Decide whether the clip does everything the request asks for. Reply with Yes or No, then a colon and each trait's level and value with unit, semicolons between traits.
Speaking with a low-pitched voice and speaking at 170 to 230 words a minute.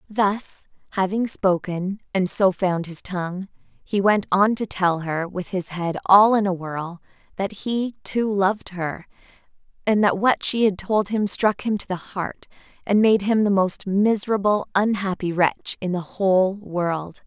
No: high, 195 Hz; average, 175 wpm